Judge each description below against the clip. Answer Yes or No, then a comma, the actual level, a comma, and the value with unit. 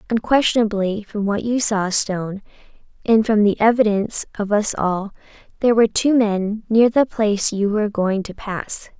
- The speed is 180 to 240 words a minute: No, average, 165 wpm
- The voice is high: Yes, high, 210 Hz